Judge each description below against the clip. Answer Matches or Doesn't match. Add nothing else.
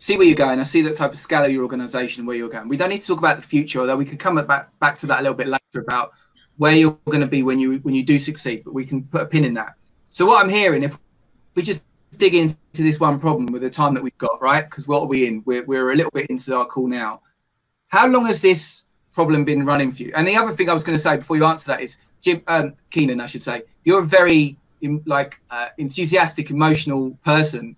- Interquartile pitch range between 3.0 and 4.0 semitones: Matches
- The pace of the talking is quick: Matches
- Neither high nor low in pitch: Matches